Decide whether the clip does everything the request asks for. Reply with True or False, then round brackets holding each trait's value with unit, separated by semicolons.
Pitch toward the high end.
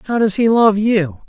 True (205 Hz)